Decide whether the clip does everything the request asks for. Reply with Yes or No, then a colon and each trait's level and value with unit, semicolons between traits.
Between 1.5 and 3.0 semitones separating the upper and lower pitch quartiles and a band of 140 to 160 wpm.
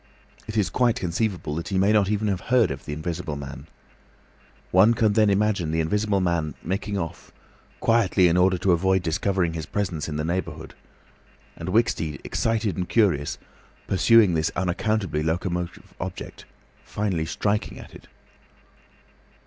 No: average, 4.1 semitones; average, 145 wpm